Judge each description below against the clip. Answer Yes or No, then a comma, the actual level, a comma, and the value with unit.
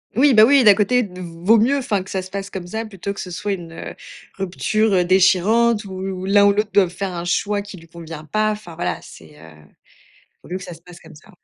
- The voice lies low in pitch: No, high, 195 Hz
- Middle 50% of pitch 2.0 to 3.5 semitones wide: Yes, average, 3.2 semitones